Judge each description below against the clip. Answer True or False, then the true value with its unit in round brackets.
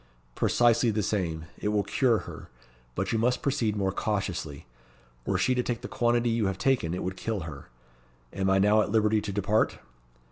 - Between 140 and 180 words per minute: False (190 wpm)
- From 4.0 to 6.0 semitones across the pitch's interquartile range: False (3.3 semitones)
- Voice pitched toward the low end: True (105 Hz)